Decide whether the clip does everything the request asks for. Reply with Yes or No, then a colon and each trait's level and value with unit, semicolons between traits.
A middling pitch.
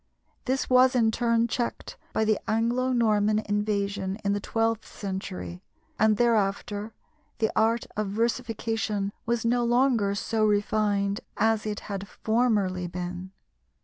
No: high, 215 Hz